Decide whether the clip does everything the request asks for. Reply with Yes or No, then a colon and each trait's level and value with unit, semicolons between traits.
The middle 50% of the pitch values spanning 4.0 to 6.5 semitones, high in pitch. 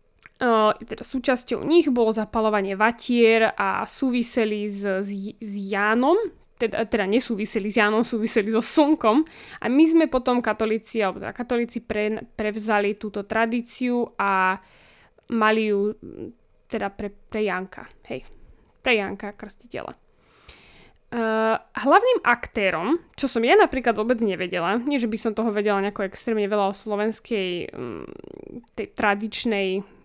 No: narrow, 2.5 semitones; high, 220 Hz